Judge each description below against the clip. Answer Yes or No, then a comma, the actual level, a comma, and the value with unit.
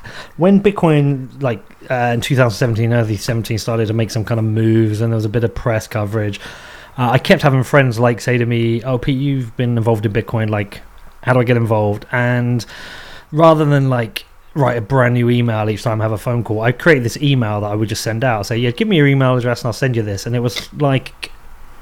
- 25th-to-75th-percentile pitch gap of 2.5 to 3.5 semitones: Yes, average, 2.8 semitones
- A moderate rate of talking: No, fast, 240 wpm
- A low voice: Yes, low, 120 Hz